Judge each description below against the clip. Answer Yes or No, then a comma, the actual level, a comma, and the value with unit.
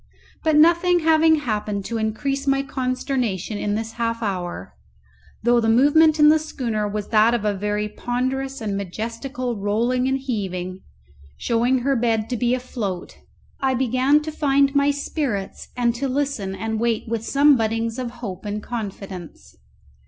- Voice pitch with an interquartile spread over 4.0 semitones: Yes, average, 4.4 semitones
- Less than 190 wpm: Yes, average, 160 wpm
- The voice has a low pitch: No, high, 235 Hz